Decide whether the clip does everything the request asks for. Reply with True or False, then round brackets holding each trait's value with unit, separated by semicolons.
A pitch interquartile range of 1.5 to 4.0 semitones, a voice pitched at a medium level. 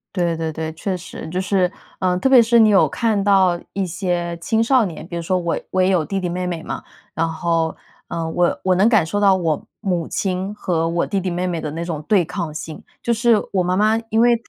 True (3.1 semitones; 180 Hz)